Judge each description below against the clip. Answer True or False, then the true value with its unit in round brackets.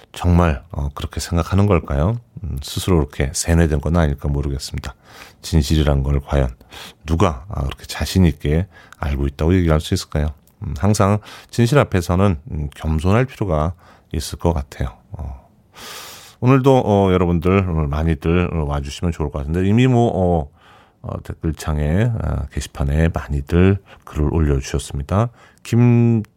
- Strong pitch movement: False (4.8 semitones)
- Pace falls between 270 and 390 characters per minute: True (285 characters per minute)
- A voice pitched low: True (85 Hz)